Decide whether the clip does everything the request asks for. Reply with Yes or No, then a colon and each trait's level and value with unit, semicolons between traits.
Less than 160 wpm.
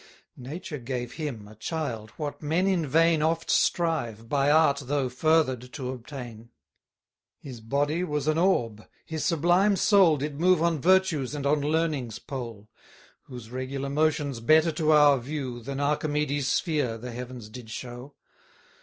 Yes: average, 150 wpm